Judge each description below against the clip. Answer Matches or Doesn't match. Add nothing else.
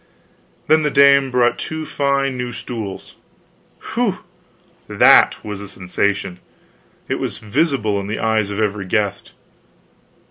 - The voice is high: Doesn't match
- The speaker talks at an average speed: Doesn't match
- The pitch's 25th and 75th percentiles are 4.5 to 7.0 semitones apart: Matches